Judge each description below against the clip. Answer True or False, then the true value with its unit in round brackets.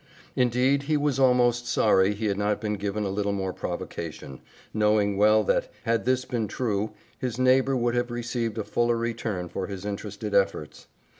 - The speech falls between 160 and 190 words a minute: True (175 wpm)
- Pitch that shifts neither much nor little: True (3.2 semitones)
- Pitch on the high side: False (110 Hz)